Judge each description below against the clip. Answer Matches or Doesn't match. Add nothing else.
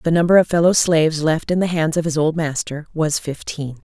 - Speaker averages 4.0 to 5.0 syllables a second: Doesn't match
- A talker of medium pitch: Matches